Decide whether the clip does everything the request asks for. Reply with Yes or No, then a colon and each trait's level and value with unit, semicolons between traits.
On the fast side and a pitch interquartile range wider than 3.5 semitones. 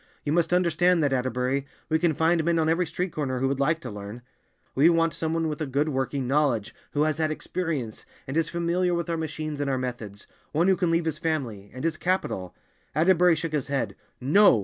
Yes: fast, 215 wpm; average, 3.9 semitones